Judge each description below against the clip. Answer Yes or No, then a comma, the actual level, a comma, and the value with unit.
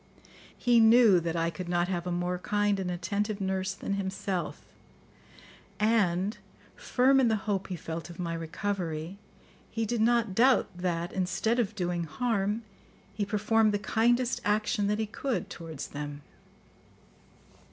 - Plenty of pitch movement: No, average, 3.9 semitones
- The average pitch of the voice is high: Yes, high, 200 Hz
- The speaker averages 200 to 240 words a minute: No, average, 150 wpm